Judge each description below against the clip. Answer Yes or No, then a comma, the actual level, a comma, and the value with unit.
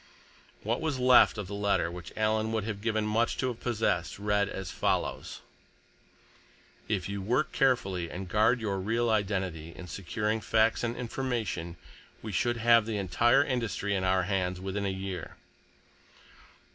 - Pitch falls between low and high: No, low, 105 Hz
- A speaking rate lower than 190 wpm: Yes, average, 160 wpm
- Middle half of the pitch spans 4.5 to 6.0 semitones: No, average, 3.5 semitones